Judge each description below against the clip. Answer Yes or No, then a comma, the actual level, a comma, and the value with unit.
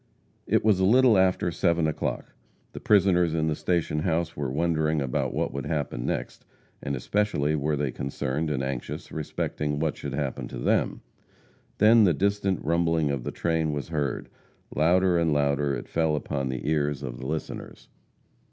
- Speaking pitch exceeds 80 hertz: No, very low, 75 Hz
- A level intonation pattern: No, average, 3.3 semitones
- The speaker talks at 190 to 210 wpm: No, average, 170 wpm